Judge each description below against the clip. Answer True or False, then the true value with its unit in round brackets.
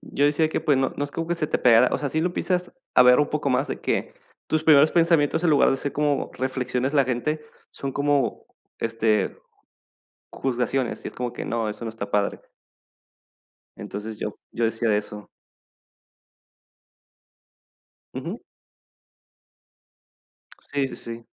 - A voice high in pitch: False (135 Hz)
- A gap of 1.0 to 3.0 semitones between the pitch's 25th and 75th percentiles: False (4.3 semitones)